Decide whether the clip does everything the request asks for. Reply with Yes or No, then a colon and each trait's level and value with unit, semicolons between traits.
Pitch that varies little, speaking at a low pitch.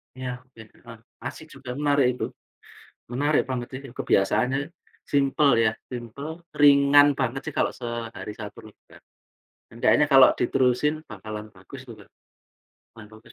No: average, 3.4 semitones; low, 130 Hz